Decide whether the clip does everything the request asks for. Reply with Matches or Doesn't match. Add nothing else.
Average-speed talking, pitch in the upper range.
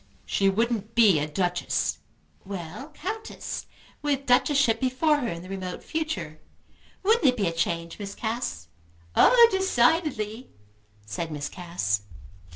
Doesn't match